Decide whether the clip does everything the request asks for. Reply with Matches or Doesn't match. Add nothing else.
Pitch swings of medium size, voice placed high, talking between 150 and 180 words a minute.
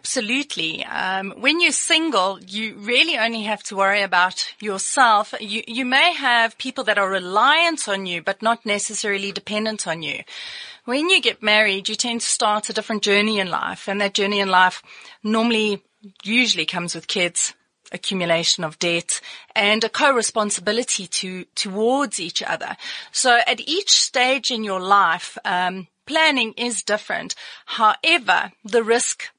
Matches